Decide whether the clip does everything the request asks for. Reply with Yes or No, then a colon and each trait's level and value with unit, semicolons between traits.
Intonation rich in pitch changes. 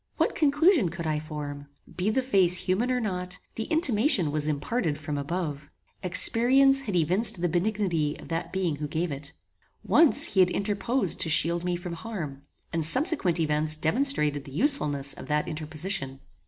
Yes: wide, 6.3 semitones